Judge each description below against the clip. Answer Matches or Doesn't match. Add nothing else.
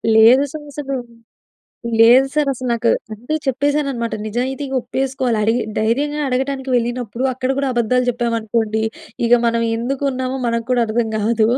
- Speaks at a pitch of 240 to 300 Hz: Matches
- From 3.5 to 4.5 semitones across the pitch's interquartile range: Doesn't match